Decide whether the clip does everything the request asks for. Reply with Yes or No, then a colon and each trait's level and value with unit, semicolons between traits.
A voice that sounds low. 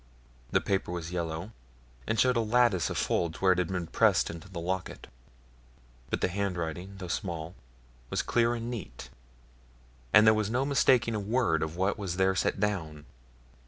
Yes: very low, 95 Hz